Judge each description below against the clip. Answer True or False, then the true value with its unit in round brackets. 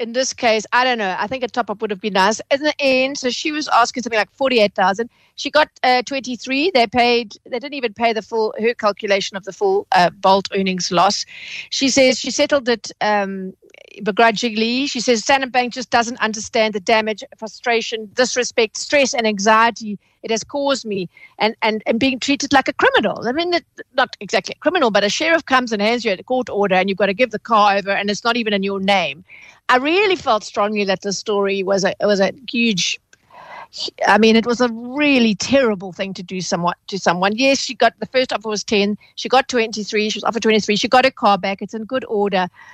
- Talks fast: True (230 wpm)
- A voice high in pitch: True (230 Hz)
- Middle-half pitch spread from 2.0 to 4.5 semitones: True (3.9 semitones)